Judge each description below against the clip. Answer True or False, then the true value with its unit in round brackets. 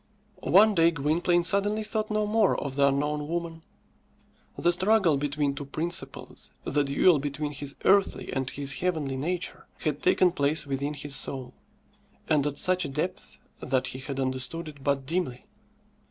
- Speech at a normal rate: True (160 wpm)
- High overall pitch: False (150 Hz)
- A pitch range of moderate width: True (4.1 semitones)